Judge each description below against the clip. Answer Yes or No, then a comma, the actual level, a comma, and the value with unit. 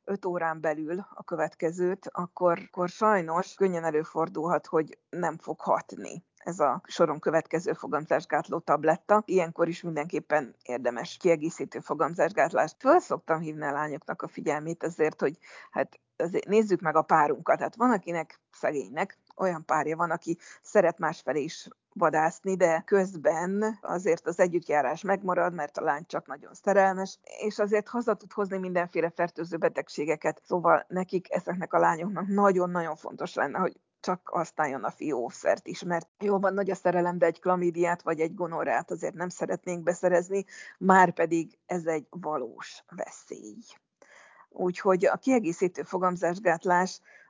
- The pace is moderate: Yes, average, 145 wpm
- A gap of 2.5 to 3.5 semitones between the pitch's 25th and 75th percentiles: Yes, average, 2.8 semitones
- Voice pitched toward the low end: No, medium, 175 Hz